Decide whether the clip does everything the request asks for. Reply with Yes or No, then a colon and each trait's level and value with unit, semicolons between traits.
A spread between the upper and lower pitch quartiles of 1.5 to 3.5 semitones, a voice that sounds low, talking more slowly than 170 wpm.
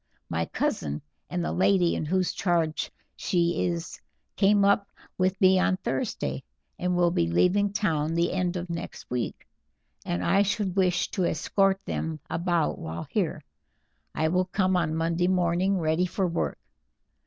No: narrow, 2.6 semitones; medium, 175 Hz; average, 155 wpm